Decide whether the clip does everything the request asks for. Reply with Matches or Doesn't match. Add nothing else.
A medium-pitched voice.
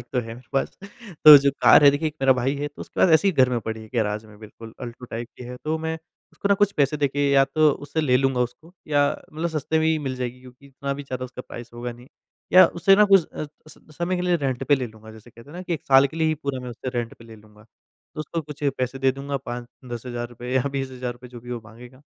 Doesn't match